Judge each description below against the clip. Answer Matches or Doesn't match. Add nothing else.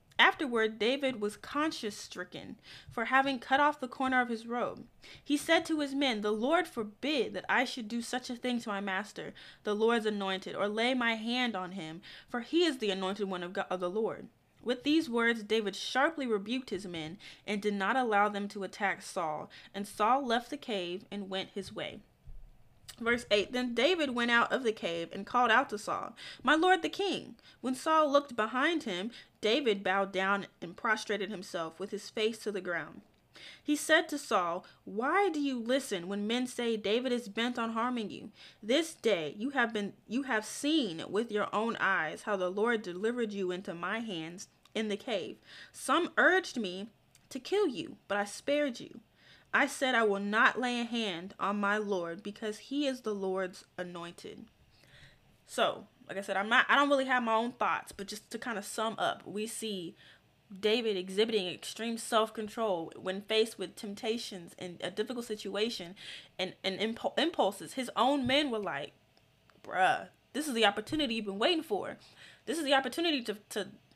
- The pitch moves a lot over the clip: Doesn't match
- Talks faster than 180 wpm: Matches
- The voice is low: Doesn't match